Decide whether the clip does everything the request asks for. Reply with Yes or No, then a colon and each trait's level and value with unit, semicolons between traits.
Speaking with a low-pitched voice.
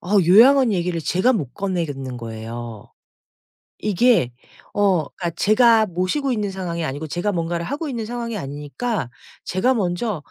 No: medium, 185 Hz